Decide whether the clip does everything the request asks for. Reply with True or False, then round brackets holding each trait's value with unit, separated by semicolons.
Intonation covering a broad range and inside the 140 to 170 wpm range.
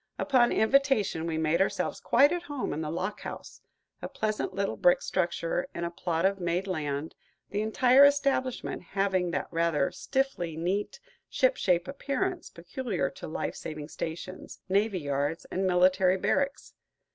True (6.5 semitones; 155 wpm)